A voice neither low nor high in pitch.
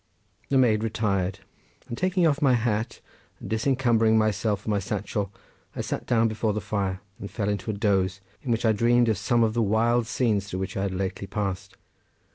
No: low, 110 Hz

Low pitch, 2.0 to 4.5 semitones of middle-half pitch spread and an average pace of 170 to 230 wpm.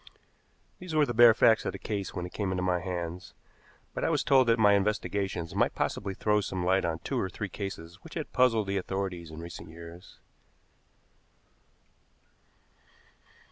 Yes: very low, 95 Hz; average, 3.4 semitones; average, 175 wpm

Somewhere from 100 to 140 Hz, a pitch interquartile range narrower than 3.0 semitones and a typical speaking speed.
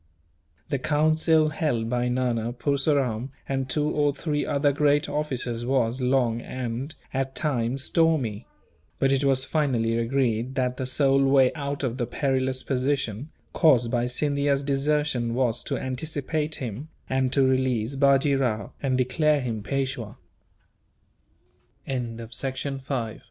No: low, 135 Hz; narrow, 2.6 semitones; slow, 130 wpm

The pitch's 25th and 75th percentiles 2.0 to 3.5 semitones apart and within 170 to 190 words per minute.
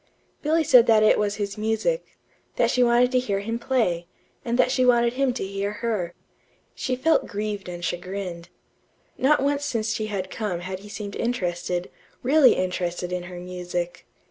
No: wide, 5.4 semitones; average, 175 wpm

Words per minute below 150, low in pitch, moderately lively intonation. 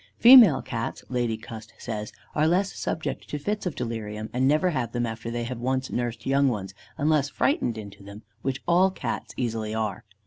No: average, 185 wpm; low, 120 Hz; average, 4.9 semitones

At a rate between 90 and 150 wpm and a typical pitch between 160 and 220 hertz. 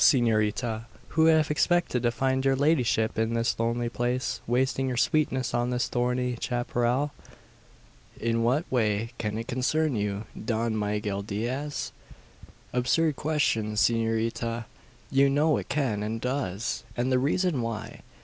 No: average, 140 wpm; low, 120 Hz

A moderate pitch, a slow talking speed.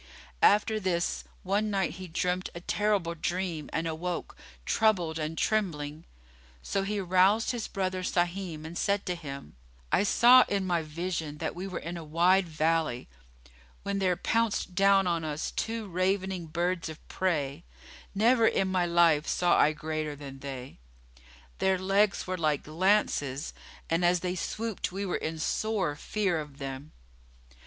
No: medium, 180 Hz; average, 155 wpm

